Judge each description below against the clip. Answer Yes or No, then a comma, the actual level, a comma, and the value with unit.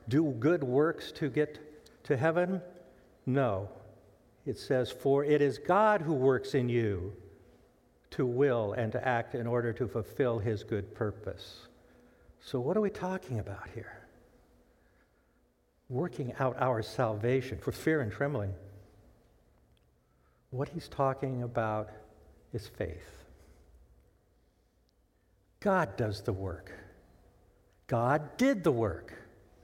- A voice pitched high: No, low, 120 Hz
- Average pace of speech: No, slow, 120 wpm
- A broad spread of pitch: Yes, wide, 6.0 semitones